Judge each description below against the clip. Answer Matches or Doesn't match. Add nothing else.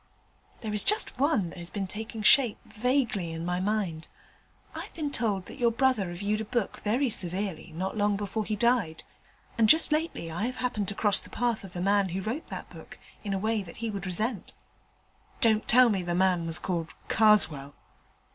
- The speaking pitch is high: Matches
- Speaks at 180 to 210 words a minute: Matches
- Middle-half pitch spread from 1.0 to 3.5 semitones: Doesn't match